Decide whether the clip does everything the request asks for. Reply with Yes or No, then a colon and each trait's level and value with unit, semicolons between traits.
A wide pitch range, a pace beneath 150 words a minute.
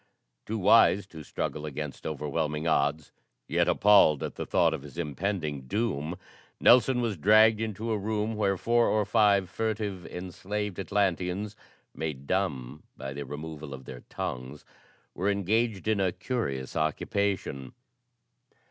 Yes: wide, 5.8 semitones; average, 140 wpm